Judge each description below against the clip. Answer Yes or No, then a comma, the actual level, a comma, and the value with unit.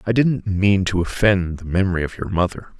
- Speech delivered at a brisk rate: Yes, fast, 215 wpm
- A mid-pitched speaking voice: No, very low, 95 Hz